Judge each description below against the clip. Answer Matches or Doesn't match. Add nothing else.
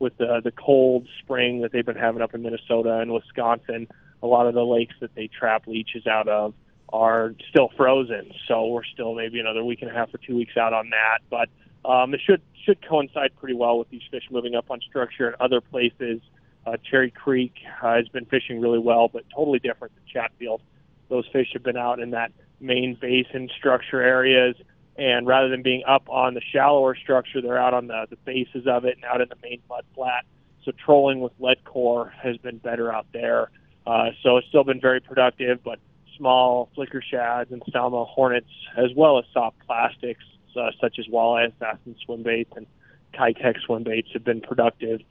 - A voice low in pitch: Matches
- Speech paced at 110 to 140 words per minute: Doesn't match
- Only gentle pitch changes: Matches